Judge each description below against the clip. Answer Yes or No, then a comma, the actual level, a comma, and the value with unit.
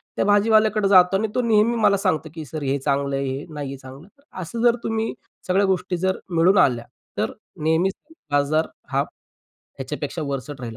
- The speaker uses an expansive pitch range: Yes, wide, 6.4 semitones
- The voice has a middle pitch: Yes, medium, 165 Hz